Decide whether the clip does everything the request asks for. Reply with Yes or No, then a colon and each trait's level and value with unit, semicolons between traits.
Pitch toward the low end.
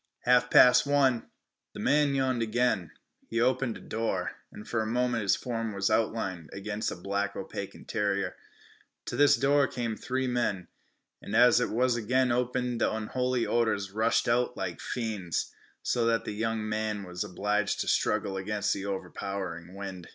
Yes: low, 110 Hz